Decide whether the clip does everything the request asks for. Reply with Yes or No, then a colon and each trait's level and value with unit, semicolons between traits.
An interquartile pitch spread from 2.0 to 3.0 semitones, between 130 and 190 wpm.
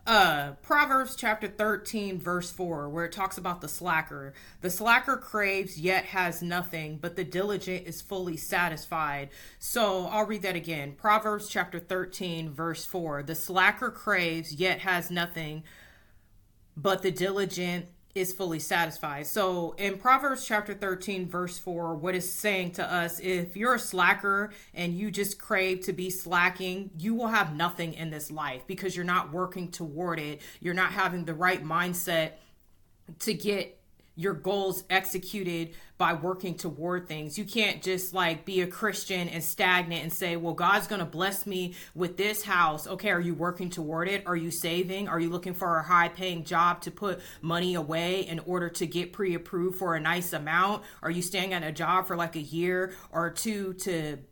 Yes: narrow, 2.4 semitones; average, 180 wpm